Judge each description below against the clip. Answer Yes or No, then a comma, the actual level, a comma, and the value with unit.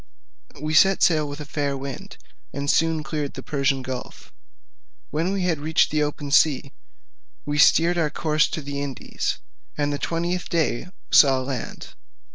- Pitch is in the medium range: Yes, medium, 150 Hz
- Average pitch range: No, narrow, 2.3 semitones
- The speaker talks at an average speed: Yes, average, 160 wpm